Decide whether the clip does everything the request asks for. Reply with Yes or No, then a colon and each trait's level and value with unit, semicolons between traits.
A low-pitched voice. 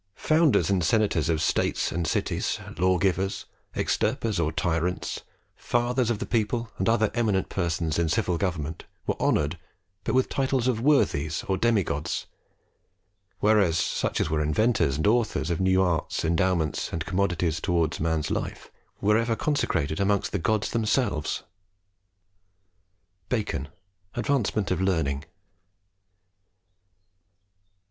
Yes: very low, 95 Hz